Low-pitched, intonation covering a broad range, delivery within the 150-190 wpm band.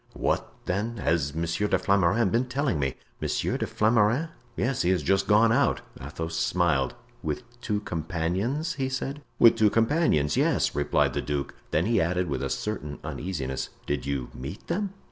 Yes: very low, 95 Hz; wide, 6.7 semitones; average, 170 wpm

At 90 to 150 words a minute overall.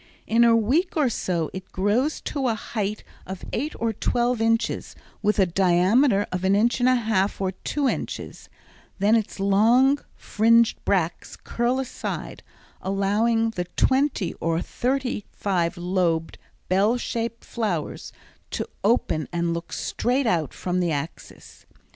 Yes: average, 145 wpm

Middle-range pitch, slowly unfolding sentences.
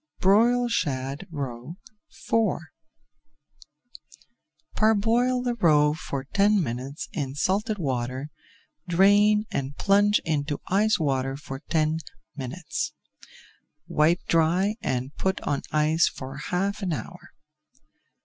Yes: medium, 160 Hz; slow, 105 wpm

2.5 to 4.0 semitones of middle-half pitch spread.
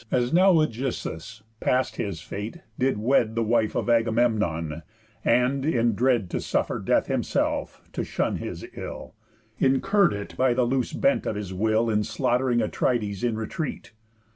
Yes: average, 3.5 semitones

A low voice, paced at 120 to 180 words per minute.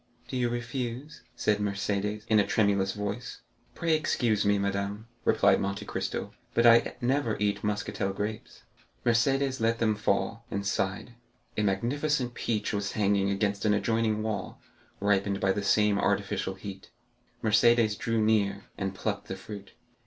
Yes: low, 105 Hz; average, 150 wpm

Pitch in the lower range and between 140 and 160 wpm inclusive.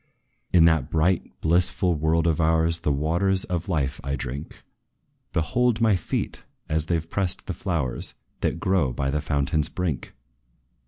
Yes: very low, 80 Hz; average, 155 wpm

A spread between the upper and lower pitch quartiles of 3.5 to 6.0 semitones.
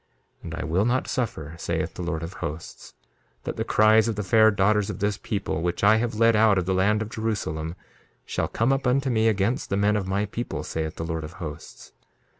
Yes: average, 4.1 semitones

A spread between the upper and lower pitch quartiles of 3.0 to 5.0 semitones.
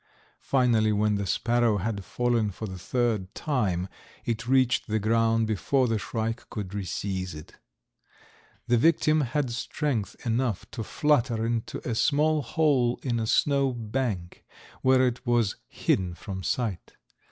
Yes: average, 3.5 semitones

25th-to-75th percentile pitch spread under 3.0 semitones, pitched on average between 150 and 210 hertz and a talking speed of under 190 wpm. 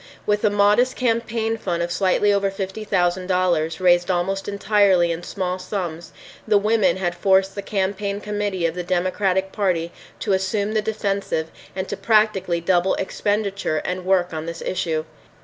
Yes: narrow, 2.6 semitones; high, 190 Hz; average, 165 wpm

